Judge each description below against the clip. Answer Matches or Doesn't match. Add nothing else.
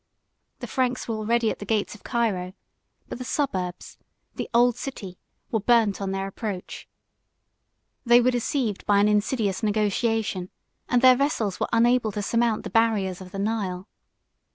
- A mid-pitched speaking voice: Doesn't match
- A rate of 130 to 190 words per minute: Matches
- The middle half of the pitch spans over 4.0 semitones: Doesn't match